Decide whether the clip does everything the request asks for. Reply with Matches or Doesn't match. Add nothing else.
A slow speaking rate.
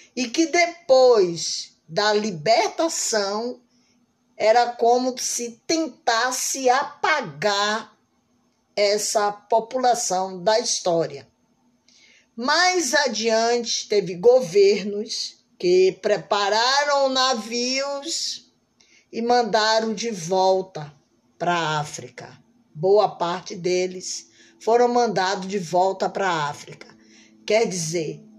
Matches